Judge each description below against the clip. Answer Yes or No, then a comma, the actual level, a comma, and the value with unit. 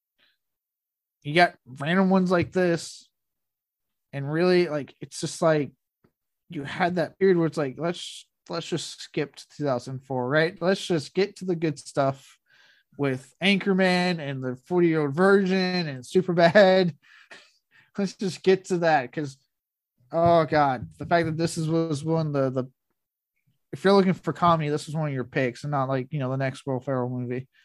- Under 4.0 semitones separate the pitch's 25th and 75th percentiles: No, average, 4.5 semitones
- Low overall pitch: No, medium, 160 Hz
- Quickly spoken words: No, average, 180 wpm